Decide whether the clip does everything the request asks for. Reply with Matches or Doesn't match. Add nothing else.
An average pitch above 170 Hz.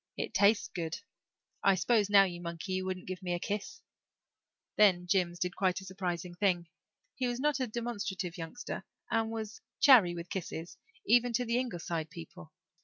Matches